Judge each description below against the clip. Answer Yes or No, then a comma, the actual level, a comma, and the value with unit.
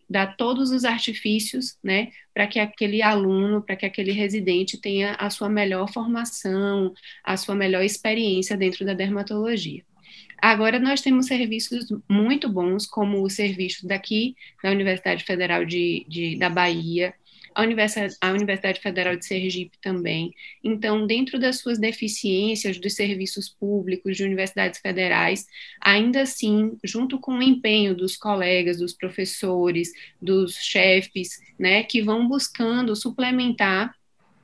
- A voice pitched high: Yes, high, 205 Hz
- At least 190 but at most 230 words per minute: No, average, 130 wpm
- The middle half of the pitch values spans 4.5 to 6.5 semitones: No, average, 2.8 semitones